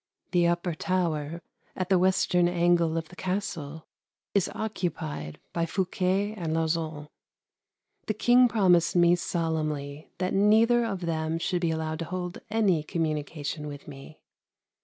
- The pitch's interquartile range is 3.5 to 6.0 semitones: No, average, 2.8 semitones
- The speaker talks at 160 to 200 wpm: No, average, 140 wpm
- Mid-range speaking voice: Yes, medium, 170 Hz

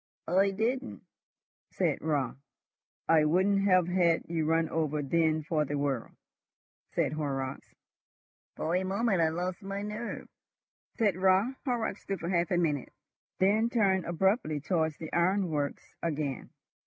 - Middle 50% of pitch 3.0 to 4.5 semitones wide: Yes, average, 4.0 semitones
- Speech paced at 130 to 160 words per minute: Yes, average, 140 wpm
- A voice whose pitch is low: No, medium, 170 Hz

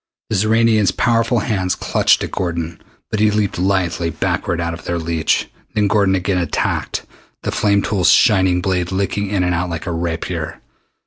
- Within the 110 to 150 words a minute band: No, average, 175 wpm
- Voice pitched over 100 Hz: No, very low, 95 Hz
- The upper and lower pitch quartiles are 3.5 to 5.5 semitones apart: No, average, 3.1 semitones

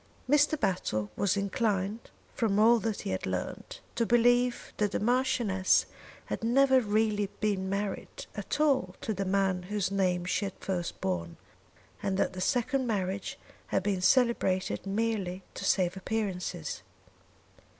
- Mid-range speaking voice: No, high, 200 Hz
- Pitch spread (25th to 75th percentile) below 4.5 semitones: Yes, average, 3.7 semitones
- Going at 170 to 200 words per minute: No, average, 145 wpm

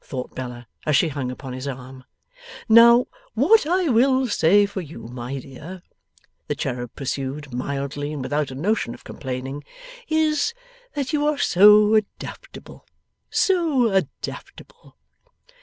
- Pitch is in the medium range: Yes, medium, 155 Hz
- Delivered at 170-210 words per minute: No, slow, 135 wpm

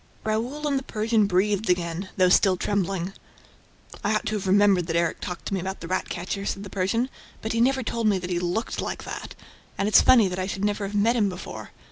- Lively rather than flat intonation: No, average, 2.9 semitones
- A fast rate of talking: Yes, fast, 235 wpm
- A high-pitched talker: Yes, high, 200 Hz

